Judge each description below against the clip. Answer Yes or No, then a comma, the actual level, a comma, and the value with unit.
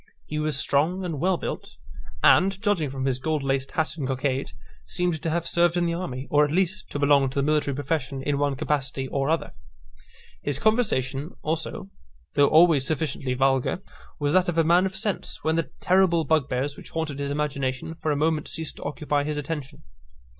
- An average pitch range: Yes, average, 3.3 semitones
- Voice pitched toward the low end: No, medium, 150 Hz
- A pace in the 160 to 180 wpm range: No, average, 195 wpm